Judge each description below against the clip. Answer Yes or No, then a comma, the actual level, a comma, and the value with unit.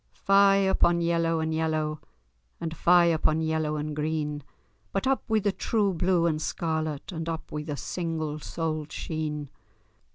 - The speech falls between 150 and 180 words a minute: Yes, average, 155 wpm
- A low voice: No, medium, 160 Hz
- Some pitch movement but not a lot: No, narrow, 2.0 semitones